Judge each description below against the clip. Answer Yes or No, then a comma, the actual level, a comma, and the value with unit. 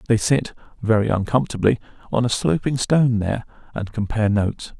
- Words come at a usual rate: Yes, average, 150 wpm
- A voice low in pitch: Yes, low, 110 Hz